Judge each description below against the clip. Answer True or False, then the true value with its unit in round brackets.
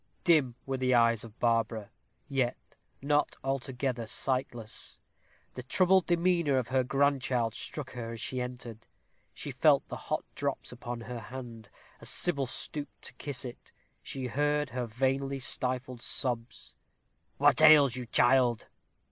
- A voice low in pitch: True (130 Hz)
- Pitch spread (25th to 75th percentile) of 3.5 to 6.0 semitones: False (2.5 semitones)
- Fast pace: False (140 wpm)